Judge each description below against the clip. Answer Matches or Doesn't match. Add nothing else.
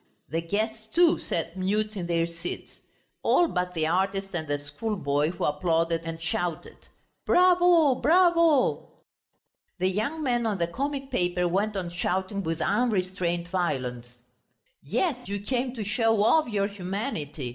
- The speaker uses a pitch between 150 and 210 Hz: Matches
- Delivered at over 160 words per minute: Doesn't match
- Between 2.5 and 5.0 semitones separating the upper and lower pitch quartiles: Doesn't match